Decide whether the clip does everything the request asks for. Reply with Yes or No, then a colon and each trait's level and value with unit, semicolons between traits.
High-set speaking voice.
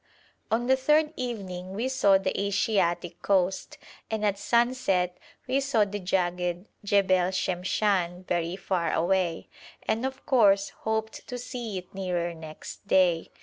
Yes: high, 195 Hz